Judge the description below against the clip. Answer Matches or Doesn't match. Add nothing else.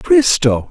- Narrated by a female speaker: Doesn't match